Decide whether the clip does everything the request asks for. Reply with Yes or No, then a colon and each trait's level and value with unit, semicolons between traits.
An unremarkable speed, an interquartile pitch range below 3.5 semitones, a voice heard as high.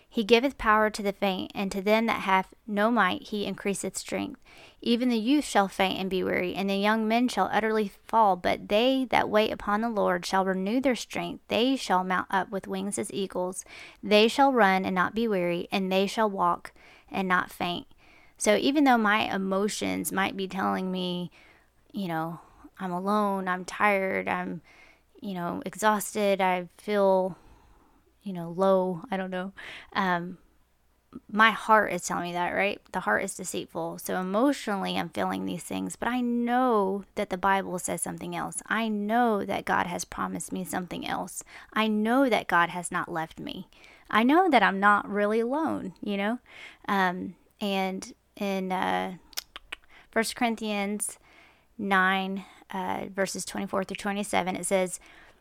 Yes: average, 170 wpm; average, 2.8 semitones; high, 195 Hz